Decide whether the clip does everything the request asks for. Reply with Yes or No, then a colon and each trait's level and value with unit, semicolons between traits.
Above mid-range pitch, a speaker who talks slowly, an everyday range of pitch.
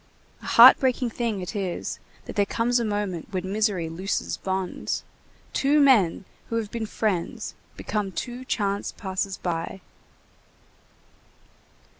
Yes: high, 205 Hz; slow, 130 wpm; average, 3.6 semitones